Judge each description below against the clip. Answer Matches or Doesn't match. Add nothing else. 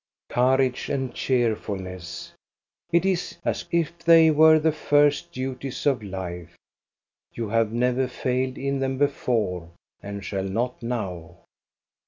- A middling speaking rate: Doesn't match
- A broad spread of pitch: Matches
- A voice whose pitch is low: Matches